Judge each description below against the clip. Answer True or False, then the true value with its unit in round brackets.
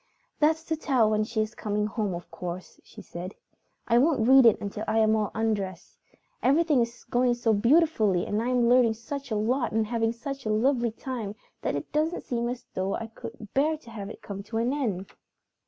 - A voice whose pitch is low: False (230 Hz)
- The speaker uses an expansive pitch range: False (3.2 semitones)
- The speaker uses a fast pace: True (210 wpm)